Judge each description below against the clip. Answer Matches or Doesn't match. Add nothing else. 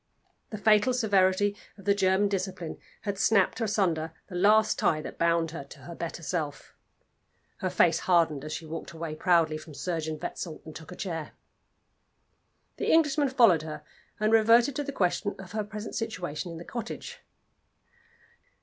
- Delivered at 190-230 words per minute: Doesn't match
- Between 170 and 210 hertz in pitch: Matches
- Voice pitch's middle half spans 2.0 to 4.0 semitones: Doesn't match